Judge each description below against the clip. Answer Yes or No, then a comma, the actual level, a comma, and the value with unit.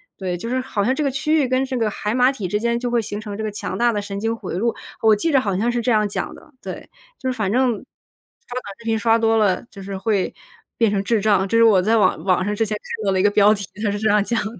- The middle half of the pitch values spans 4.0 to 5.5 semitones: No, average, 2.7 semitones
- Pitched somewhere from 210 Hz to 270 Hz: Yes, high, 220 Hz